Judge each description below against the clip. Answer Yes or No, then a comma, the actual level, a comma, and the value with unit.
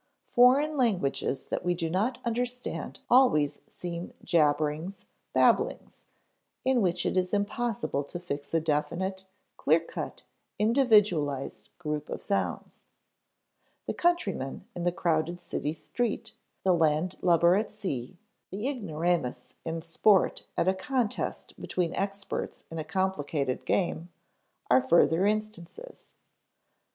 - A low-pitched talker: No, medium, 180 Hz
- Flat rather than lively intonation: No, average, 5.2 semitones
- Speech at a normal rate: No, slow, 120 wpm